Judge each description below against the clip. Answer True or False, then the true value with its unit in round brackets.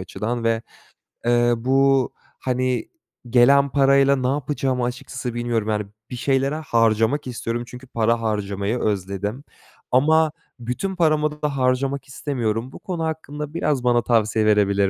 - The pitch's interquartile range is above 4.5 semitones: False (3.4 semitones)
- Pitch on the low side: True (125 Hz)